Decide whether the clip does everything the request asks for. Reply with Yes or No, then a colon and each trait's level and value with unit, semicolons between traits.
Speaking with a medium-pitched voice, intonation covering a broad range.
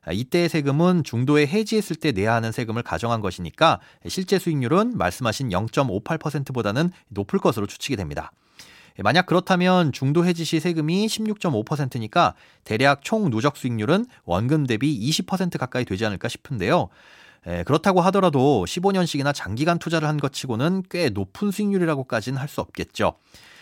Yes: medium, 150 Hz; wide, 7.3 semitones